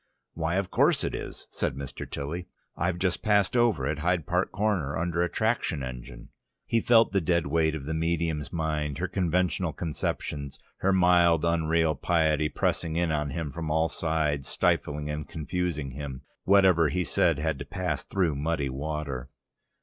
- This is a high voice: No, very low, 80 Hz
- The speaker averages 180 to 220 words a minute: No, average, 170 wpm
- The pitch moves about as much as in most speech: Yes, average, 3.1 semitones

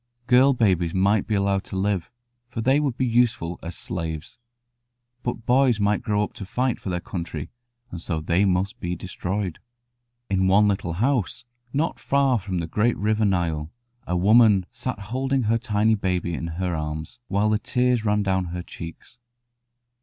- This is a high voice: No, low, 100 Hz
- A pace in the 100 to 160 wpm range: No, average, 175 wpm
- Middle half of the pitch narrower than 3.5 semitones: No, average, 4.7 semitones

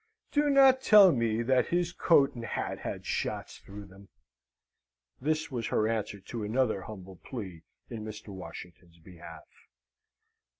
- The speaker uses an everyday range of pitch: No, wide, 6.2 semitones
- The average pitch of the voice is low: Yes, low, 110 Hz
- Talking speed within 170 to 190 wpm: No, average, 140 wpm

